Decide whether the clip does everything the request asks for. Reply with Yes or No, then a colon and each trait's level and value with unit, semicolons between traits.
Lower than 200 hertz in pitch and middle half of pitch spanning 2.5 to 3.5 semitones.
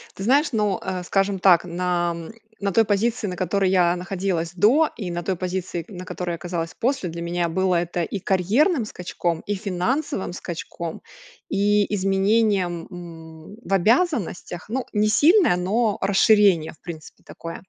Yes: high, 190 Hz; average, 3.2 semitones